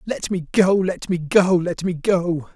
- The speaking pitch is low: No, medium, 180 Hz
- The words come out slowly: No, fast, 210 wpm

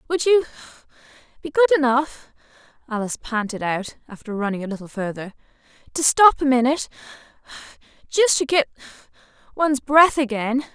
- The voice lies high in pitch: Yes, very high, 265 Hz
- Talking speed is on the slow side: Yes, slow, 110 wpm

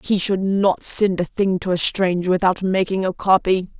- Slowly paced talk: No, fast, 205 wpm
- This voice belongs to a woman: Yes, female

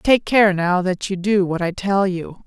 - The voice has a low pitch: No, high, 190 Hz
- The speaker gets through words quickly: Yes, fast, 245 wpm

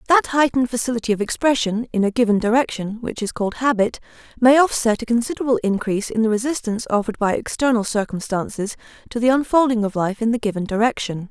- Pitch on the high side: Yes, high, 230 Hz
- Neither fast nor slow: Yes, average, 180 wpm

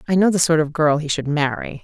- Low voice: No, medium, 155 Hz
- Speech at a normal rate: No, fast, 295 wpm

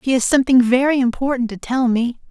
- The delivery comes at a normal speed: No, fast, 210 wpm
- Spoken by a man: No, female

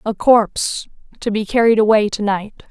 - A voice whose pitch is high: Yes, high, 215 Hz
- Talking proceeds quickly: No, average, 175 wpm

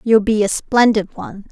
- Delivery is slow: No, average, 200 wpm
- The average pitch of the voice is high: Yes, high, 215 Hz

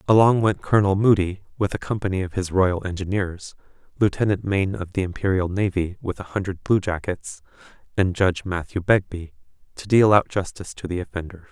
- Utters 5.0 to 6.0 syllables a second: Yes, 5.8 syllables/s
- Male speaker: Yes, male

